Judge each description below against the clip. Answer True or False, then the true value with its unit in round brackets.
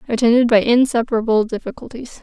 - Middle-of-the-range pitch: False (230 Hz)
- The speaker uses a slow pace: True (110 wpm)